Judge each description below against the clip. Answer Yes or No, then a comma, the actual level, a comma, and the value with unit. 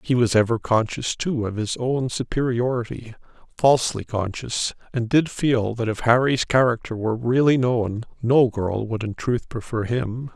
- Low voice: Yes, low, 120 Hz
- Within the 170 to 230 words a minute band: No, average, 150 wpm